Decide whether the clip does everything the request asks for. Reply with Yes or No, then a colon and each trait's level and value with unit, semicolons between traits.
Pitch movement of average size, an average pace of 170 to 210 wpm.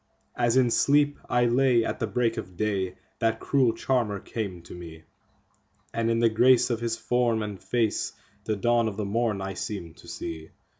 Yes: average, 3.3 semitones; average, 185 wpm